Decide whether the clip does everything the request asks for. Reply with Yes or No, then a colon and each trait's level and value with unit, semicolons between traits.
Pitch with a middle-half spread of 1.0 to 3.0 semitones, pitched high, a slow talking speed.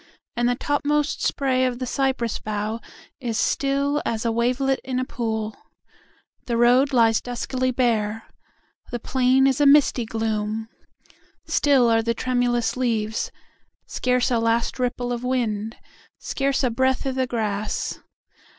Yes: narrow, 2.5 semitones; high, 245 Hz; slow, 120 wpm